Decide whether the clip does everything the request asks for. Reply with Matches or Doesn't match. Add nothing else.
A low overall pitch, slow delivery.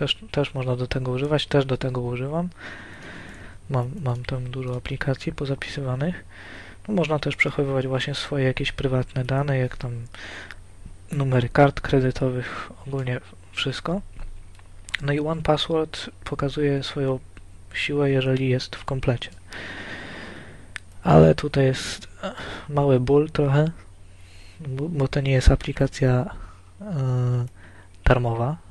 Doesn't match